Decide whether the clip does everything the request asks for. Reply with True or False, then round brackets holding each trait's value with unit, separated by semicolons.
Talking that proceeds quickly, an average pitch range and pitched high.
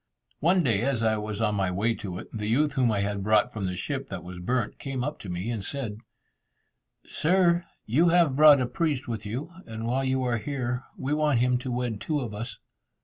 False (225 wpm; 4.8 semitones; 120 Hz)